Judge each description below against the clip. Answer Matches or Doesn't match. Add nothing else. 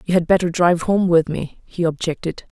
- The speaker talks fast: Matches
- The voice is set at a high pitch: Doesn't match